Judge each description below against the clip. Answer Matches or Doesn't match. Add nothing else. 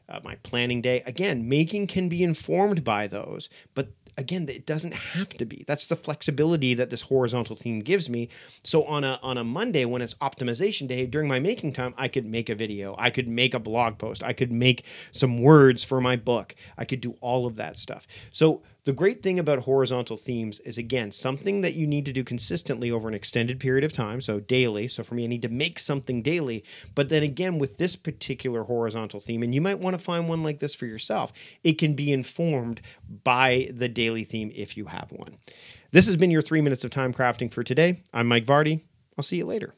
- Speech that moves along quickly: Matches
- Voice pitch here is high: Doesn't match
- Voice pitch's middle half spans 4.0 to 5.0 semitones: Matches